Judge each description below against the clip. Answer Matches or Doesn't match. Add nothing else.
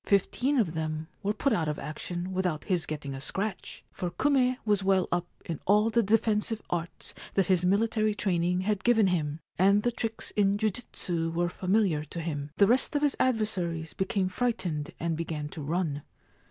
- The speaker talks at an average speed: Matches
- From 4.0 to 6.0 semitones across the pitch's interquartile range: Matches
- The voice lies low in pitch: Doesn't match